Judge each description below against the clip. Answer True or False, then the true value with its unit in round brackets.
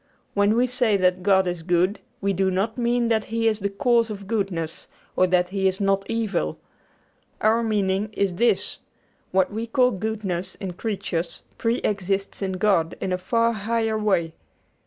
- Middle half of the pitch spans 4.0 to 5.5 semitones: False (3.3 semitones)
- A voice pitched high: True (200 Hz)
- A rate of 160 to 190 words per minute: True (170 wpm)